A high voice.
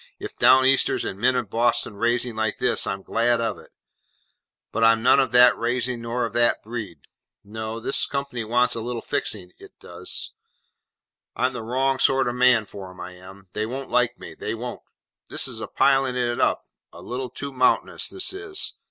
No: low, 120 Hz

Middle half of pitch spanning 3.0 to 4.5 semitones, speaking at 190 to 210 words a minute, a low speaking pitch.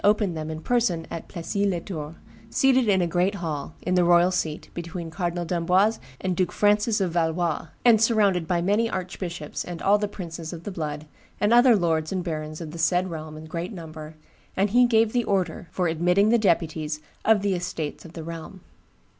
No: average, 3.6 semitones; average, 200 wpm; medium, 175 Hz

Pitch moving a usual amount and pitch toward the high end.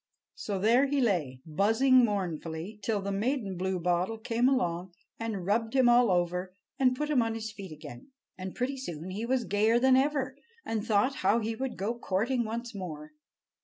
Yes: average, 4.9 semitones; high, 220 Hz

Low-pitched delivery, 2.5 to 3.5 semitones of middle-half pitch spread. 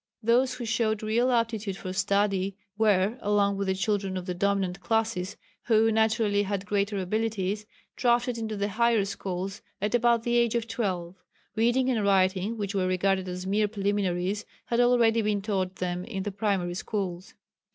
No: high, 205 Hz; average, 2.8 semitones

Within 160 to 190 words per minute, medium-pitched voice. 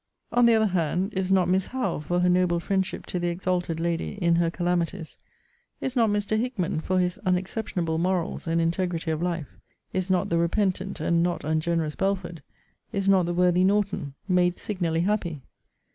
Yes: average, 175 wpm; medium, 180 Hz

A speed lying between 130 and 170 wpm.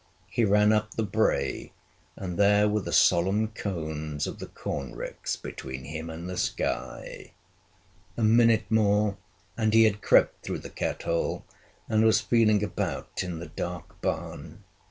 Yes: average, 155 wpm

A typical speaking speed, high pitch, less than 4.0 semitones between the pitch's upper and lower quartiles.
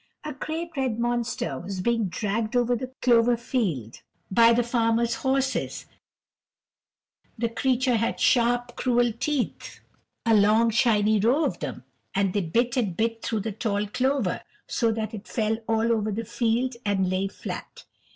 Yes: average, 155 wpm; high, 230 Hz; narrow, 2.4 semitones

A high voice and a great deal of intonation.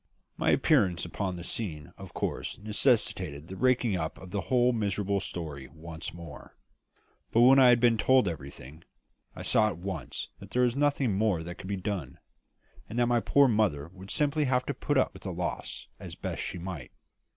No: low, 100 Hz; wide, 6.1 semitones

